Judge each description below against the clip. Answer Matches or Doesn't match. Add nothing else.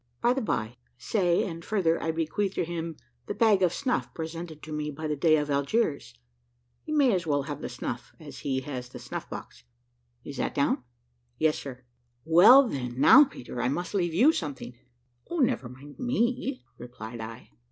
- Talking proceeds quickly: Doesn't match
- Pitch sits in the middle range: Matches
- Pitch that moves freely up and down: Matches